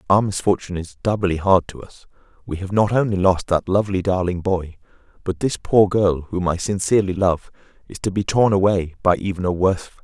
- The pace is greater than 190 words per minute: Yes, fast, 205 wpm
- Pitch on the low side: Yes, very low, 95 Hz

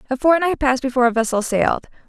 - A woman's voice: Yes, female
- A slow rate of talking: No, average, 200 wpm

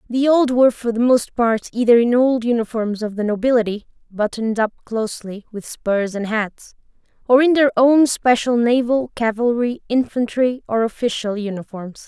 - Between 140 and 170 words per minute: Yes, average, 160 wpm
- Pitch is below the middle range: No, high, 235 Hz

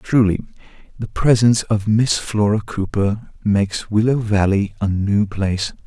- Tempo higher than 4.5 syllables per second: No, 4.4 syllables/s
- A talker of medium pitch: No, low, 105 Hz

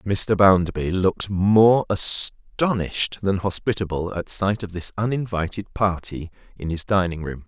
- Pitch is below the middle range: Yes, very low, 95 Hz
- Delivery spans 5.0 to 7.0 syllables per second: No, 4.4 syllables/s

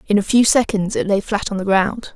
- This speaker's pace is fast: Yes, fast, 280 wpm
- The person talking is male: No, female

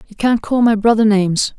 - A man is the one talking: No, female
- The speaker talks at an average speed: No, fast, 225 wpm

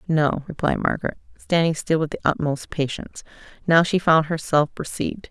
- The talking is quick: No, average, 160 wpm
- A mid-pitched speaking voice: Yes, medium, 160 Hz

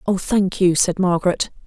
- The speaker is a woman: Yes, female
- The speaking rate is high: No, average, 180 wpm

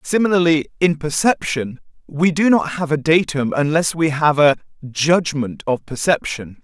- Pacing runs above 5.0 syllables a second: No, 4.5 syllables/s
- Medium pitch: Yes, medium, 155 Hz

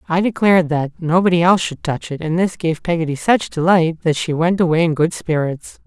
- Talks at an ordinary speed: No, fast, 215 wpm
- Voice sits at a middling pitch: Yes, medium, 170 Hz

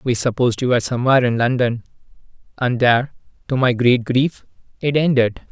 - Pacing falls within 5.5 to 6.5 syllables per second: Yes, 6.0 syllables/s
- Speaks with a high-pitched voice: No, low, 125 Hz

